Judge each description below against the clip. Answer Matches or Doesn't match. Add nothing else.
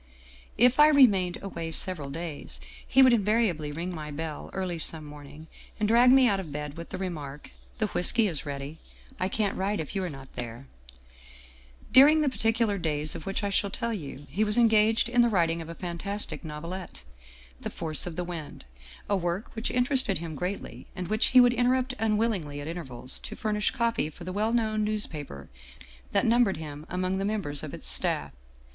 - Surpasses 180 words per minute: Matches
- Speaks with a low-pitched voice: Doesn't match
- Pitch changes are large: Matches